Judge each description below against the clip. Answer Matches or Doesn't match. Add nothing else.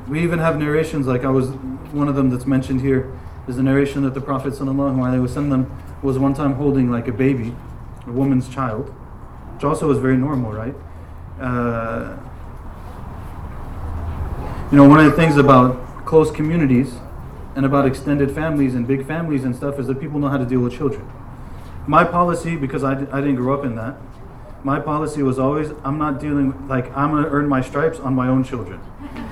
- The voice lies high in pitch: Doesn't match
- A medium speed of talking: Matches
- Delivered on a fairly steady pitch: Matches